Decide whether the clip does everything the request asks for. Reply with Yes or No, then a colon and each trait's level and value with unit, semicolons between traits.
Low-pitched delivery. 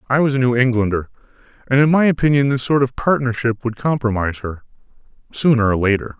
Yes: low, 125 Hz